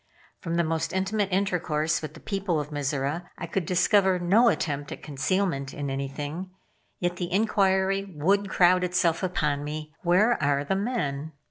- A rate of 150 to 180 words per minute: Yes, average, 160 wpm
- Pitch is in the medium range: Yes, medium, 175 Hz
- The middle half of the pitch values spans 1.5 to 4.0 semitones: No, average, 4.4 semitones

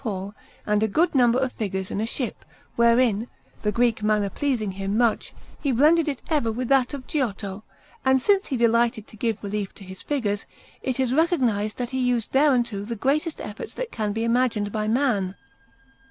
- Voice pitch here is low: No, high, 235 Hz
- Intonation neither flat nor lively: Yes, average, 4.0 semitones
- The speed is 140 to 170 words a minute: No, average, 190 wpm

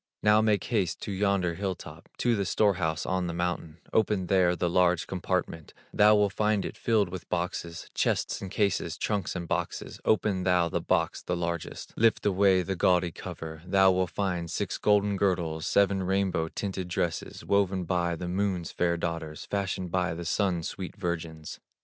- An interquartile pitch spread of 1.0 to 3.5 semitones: Yes, narrow, 2.5 semitones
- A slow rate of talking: No, average, 180 wpm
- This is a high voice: No, very low, 90 Hz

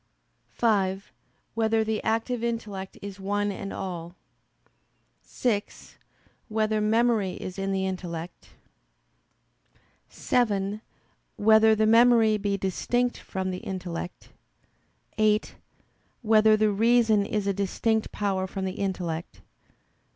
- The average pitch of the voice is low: No, high, 205 Hz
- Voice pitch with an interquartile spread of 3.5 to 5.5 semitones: No, narrow, 2.5 semitones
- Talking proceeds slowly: Yes, slow, 105 wpm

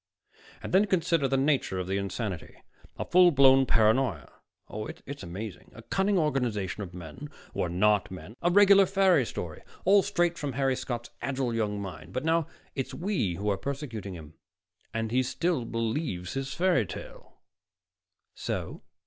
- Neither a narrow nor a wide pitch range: No, wide, 8.2 semitones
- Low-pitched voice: Yes, low, 130 Hz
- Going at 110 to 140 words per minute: No, average, 165 wpm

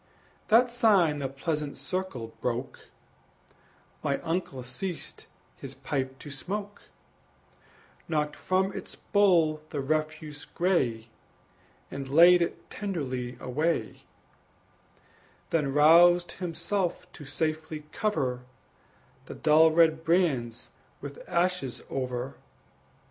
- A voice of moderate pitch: Yes, medium, 155 Hz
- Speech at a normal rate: No, slow, 100 wpm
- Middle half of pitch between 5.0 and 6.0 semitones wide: No, average, 4.6 semitones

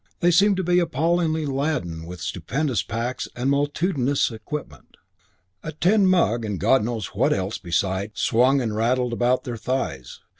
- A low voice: Yes, low, 130 Hz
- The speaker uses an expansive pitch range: Yes, wide, 6.2 semitones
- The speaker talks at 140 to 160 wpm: Yes, average, 155 wpm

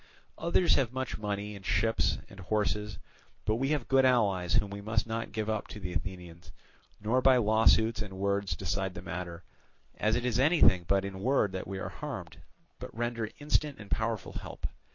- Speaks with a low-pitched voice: Yes, low, 105 Hz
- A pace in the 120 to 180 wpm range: No, average, 190 wpm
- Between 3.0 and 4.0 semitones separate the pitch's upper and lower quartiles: Yes, average, 3.4 semitones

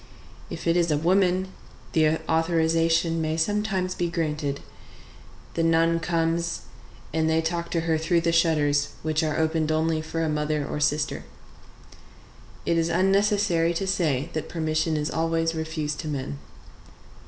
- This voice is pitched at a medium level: Yes, medium, 165 Hz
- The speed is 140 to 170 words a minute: Yes, average, 150 wpm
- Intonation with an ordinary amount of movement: No, narrow, 1.3 semitones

